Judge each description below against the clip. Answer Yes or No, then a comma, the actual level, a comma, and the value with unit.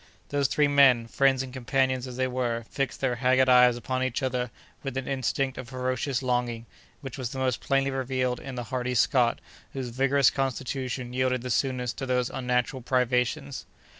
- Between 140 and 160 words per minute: No, average, 175 wpm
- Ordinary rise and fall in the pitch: No, narrow, 1.2 semitones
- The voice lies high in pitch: No, low, 130 Hz